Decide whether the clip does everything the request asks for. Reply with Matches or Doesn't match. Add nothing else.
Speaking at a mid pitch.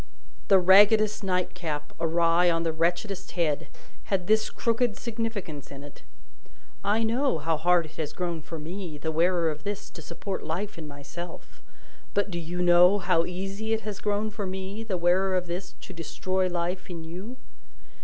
Matches